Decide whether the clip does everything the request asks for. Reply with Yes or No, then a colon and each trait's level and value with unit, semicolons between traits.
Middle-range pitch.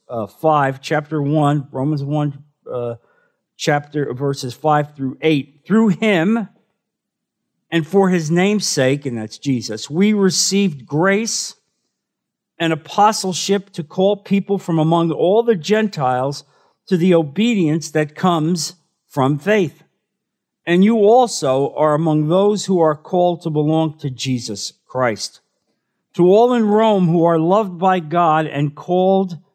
Yes: medium, 165 Hz